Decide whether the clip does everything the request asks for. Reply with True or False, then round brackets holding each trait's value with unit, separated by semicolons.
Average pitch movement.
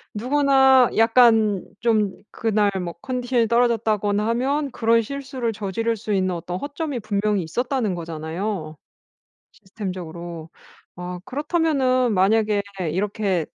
True (4.8 semitones)